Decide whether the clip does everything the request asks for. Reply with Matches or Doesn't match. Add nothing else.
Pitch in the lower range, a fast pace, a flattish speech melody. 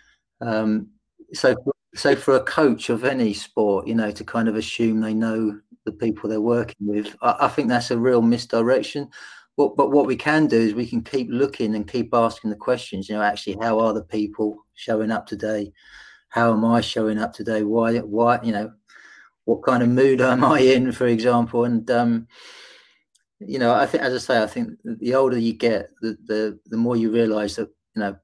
Matches